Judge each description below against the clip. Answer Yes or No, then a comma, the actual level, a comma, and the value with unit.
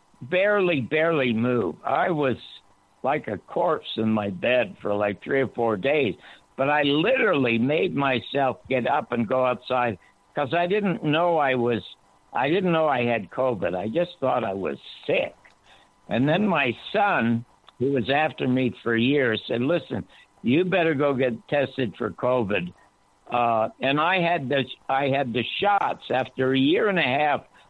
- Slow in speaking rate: No, average, 170 wpm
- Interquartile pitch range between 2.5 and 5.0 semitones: Yes, average, 3.8 semitones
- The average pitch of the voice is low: Yes, low, 130 Hz